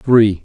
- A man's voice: Yes, male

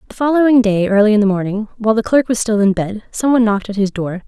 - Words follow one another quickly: Yes, fast, 265 wpm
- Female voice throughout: Yes, female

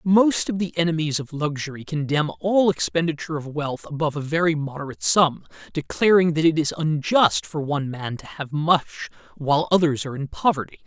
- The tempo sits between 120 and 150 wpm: No, average, 175 wpm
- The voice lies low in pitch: No, medium, 155 Hz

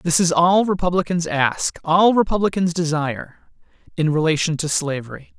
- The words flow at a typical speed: No, slow, 110 wpm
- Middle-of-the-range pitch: Yes, medium, 165 Hz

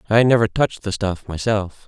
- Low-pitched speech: Yes, low, 105 Hz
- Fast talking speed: No, average, 190 wpm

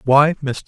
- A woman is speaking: No, male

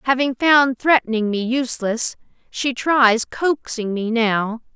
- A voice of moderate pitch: No, high, 245 Hz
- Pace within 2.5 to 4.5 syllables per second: Yes, 4.1 syllables/s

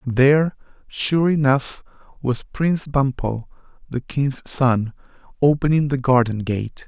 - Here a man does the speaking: Yes, male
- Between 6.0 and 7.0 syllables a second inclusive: No, 4.1 syllables/s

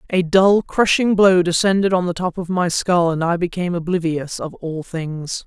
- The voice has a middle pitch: Yes, medium, 175 Hz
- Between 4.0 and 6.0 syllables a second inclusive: Yes, 4.8 syllables/s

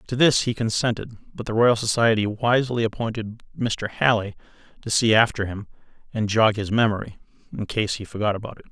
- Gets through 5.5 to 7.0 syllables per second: Yes, 5.8 syllables/s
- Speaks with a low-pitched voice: Yes, low, 110 Hz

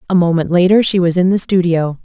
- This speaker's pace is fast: Yes, fast, 235 wpm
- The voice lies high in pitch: No, medium, 180 Hz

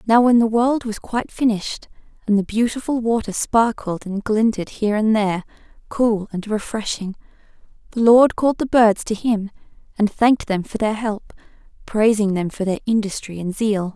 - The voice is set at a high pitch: Yes, high, 215 Hz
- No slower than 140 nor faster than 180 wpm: Yes, average, 170 wpm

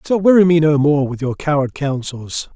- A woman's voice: No, male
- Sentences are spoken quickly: Yes, fast, 210 wpm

